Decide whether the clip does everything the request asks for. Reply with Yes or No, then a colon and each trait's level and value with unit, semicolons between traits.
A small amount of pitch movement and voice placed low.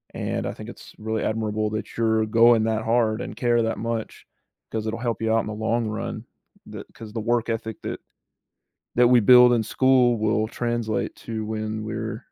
Yes: narrow, 1.4 semitones; low, 110 Hz